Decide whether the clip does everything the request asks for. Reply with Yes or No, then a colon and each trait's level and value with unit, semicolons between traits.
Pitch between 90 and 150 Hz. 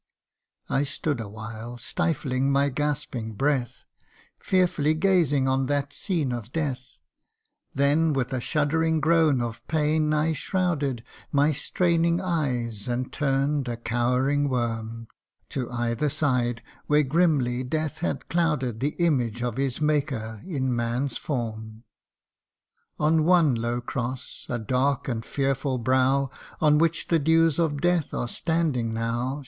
Yes: low, 135 Hz